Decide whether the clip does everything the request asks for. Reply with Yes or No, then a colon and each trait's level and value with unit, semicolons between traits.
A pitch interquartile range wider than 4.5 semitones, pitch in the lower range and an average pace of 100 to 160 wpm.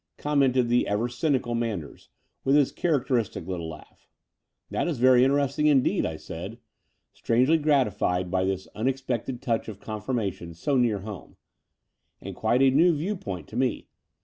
Yes: average, 5.3 semitones; low, 120 Hz; average, 155 wpm